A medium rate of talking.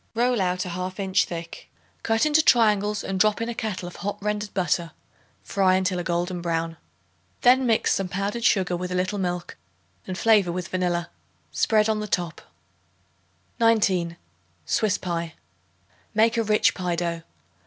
Yes: average, 165 wpm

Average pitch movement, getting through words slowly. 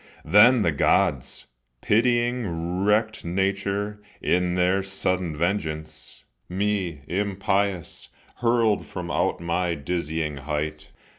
Yes: average, 3.8 semitones; slow, 95 wpm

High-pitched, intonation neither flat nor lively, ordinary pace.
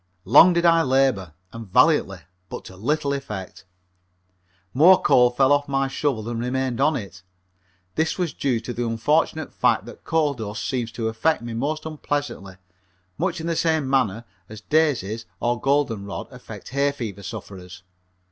No: low, 130 Hz; average, 4.9 semitones; average, 165 wpm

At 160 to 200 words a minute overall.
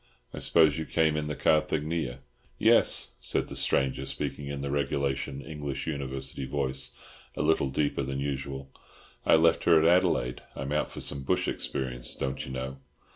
Yes: average, 170 wpm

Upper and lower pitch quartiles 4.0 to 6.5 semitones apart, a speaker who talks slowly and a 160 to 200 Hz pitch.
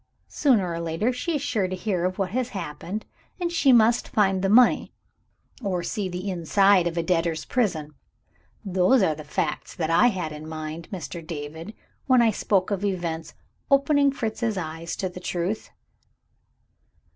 No: average, 4.9 semitones; average, 170 wpm; medium, 185 Hz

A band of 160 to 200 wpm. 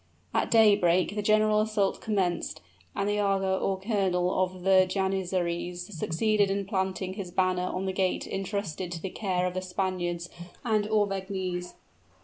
No: average, 150 wpm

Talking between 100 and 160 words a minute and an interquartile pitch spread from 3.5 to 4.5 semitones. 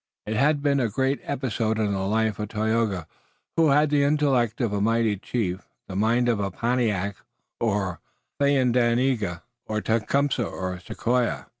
Yes: average, 150 wpm; average, 4.1 semitones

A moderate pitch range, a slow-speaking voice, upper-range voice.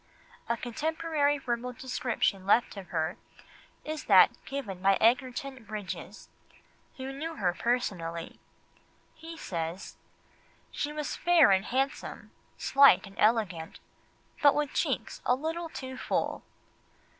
No: wide, 6.6 semitones; slow, 120 wpm; very high, 250 Hz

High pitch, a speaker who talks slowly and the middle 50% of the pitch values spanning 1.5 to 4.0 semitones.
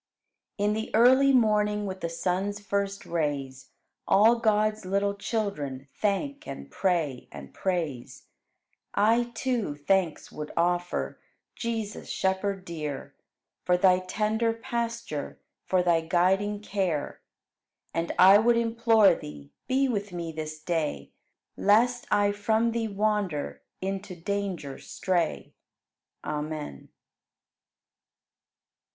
No: high, 195 Hz; slow, 110 wpm; average, 4.5 semitones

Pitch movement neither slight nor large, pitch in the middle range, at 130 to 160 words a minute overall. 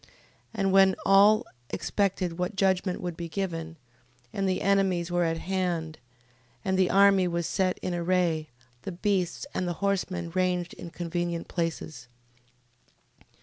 No: narrow, 2.1 semitones; medium, 180 Hz; average, 150 wpm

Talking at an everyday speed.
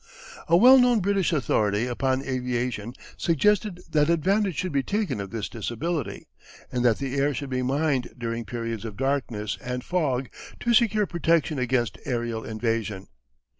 Yes: average, 155 wpm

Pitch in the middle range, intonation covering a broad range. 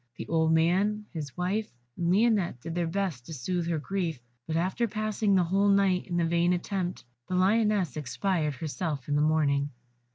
No: medium, 175 Hz; average, 3.6 semitones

